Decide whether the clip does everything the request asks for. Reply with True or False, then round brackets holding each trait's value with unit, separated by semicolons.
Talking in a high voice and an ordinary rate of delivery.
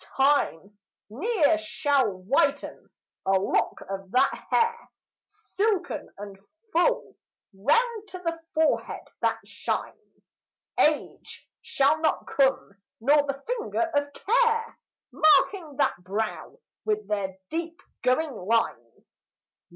False (290 Hz; 105 wpm)